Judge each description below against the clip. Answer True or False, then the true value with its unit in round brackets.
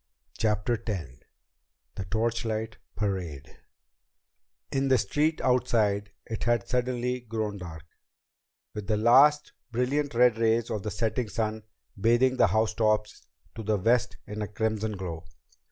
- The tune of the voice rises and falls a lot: False (2.5 semitones)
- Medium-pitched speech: False (110 Hz)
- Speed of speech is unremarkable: False (130 wpm)